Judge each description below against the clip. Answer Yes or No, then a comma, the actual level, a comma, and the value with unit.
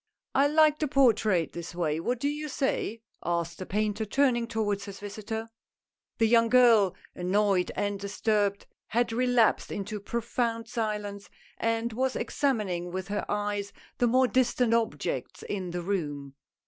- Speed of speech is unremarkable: Yes, average, 155 wpm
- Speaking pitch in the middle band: No, high, 215 Hz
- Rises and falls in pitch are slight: No, average, 3.3 semitones